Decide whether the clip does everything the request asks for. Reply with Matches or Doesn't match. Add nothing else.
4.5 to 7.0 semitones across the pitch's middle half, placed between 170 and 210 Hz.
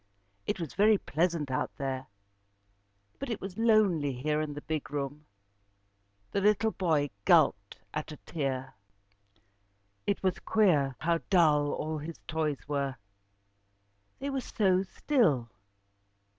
Doesn't match